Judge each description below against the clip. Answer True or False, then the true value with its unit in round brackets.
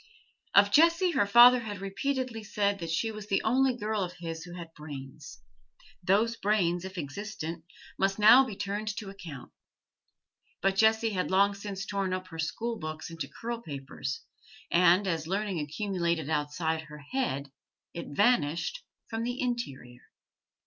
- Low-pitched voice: False (195 Hz)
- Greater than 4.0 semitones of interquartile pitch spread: True (5.1 semitones)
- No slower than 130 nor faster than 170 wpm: True (155 wpm)